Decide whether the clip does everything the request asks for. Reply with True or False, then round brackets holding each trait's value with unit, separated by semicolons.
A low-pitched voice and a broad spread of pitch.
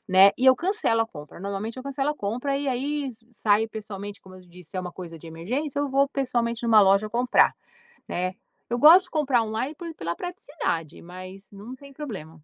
False (225 Hz; 6.4 semitones)